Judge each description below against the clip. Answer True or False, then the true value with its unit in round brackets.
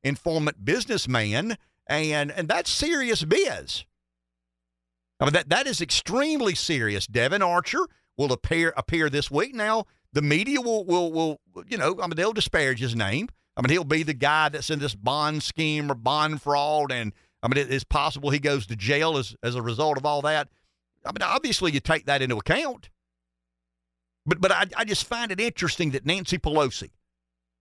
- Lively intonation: True (6.6 semitones)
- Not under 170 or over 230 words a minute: True (185 wpm)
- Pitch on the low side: False (150 Hz)